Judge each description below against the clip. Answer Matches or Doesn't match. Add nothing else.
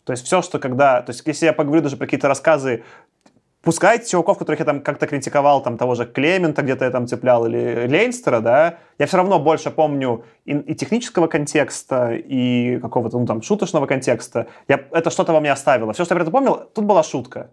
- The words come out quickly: Matches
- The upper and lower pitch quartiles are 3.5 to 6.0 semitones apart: Matches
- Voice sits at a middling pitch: Matches